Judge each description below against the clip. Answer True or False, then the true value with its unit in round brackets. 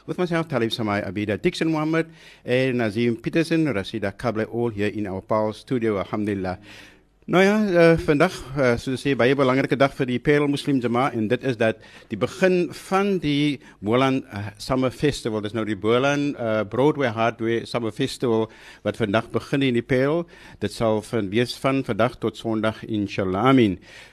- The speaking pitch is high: False (120 Hz)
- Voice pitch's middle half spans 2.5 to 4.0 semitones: False (4.7 semitones)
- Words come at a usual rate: True (180 wpm)